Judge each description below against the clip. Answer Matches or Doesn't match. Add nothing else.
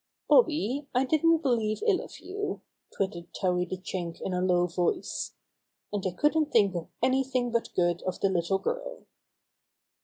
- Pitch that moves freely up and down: Matches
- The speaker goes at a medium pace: Matches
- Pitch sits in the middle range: Doesn't match